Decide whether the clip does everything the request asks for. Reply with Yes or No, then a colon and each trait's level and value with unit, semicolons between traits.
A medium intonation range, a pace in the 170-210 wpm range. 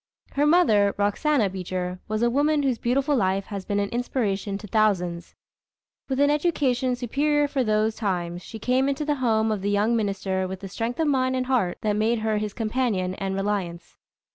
Yes: average, 4.9 semitones; average, 190 wpm